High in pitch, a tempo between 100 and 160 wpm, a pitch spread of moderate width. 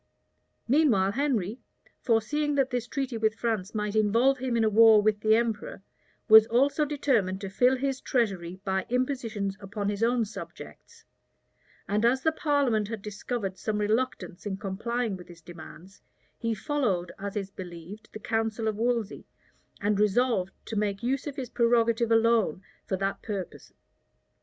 Yes: high, 220 Hz; average, 155 wpm; average, 3.6 semitones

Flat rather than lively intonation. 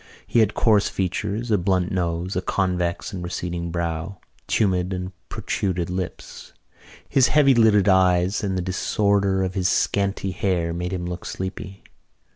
Yes: narrow, 2.0 semitones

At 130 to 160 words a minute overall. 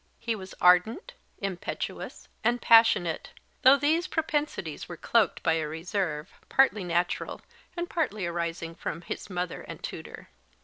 Yes: average, 140 wpm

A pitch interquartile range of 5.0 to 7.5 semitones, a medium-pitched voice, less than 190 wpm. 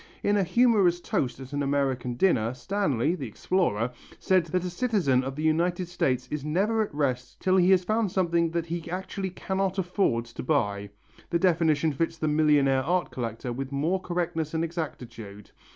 Yes: wide, 5.6 semitones; medium, 160 Hz; average, 180 wpm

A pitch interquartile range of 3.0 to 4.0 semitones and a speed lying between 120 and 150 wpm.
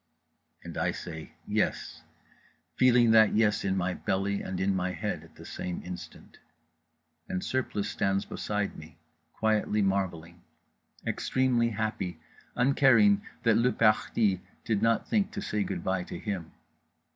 Yes: average, 3.7 semitones; average, 145 wpm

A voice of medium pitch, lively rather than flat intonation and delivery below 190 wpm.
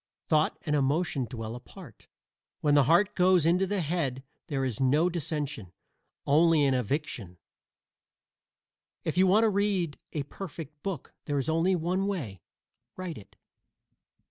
No: medium, 155 Hz; average, 4.9 semitones; average, 145 wpm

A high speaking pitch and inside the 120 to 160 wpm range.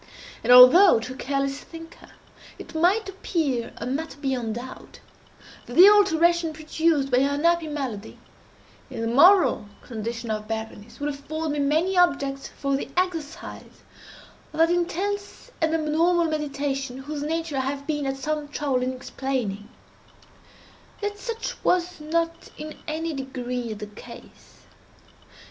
Yes: very high, 290 Hz; average, 140 wpm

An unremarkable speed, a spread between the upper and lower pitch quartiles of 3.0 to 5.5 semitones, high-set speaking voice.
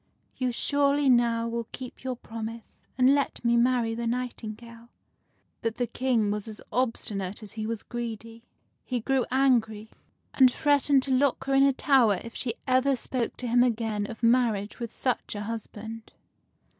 No: average, 170 wpm; narrow, 2.4 semitones; high, 235 Hz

